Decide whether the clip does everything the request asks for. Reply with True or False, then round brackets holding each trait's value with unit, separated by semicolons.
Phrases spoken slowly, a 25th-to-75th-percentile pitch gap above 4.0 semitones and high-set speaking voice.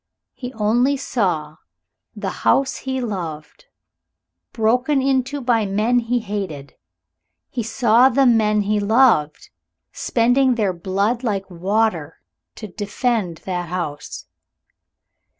True (110 wpm; 4.8 semitones; 220 Hz)